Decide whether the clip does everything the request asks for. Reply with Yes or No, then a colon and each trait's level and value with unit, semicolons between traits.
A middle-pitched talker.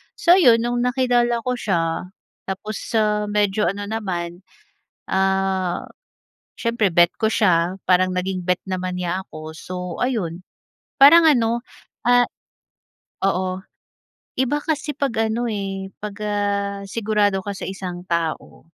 No: high, 200 Hz